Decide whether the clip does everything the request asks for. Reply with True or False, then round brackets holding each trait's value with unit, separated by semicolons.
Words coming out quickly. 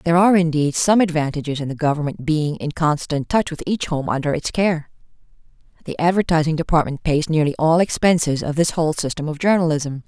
False (185 wpm)